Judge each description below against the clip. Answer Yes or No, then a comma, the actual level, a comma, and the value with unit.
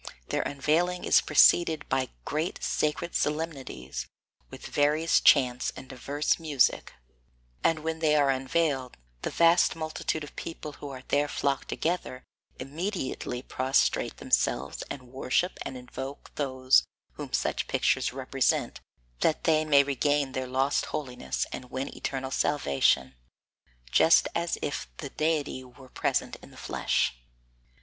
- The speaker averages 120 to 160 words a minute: Yes, slow, 135 wpm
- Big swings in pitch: No, average, 3.3 semitones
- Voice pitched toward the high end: No, medium, 140 Hz